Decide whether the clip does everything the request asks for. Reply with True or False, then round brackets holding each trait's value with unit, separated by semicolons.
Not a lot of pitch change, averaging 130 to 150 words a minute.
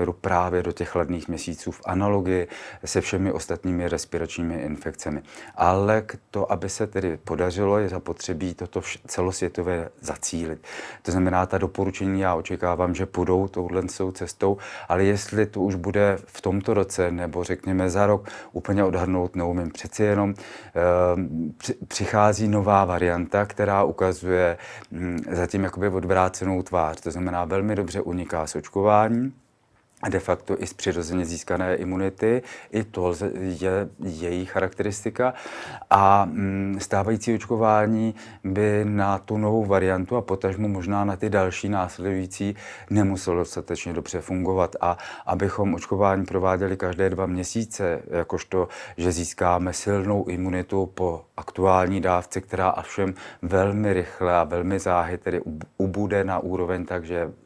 True (2.0 semitones; 135 wpm)